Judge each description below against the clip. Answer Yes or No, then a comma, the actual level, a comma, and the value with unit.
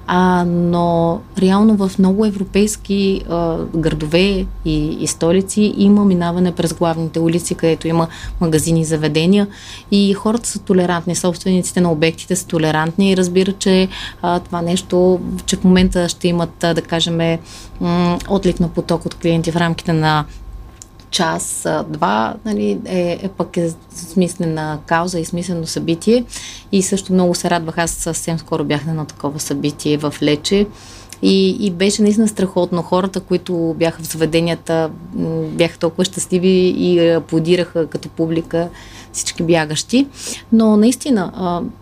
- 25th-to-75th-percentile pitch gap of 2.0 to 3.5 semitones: Yes, narrow, 2.4 semitones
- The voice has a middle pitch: Yes, medium, 175 Hz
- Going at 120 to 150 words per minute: Yes, average, 145 wpm